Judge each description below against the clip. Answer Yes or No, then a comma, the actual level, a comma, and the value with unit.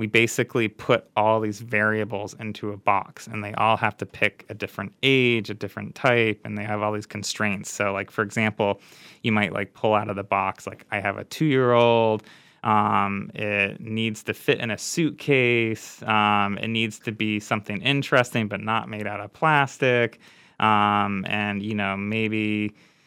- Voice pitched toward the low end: Yes, low, 110 Hz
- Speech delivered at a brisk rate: No, average, 180 wpm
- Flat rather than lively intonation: Yes, narrow, 1.6 semitones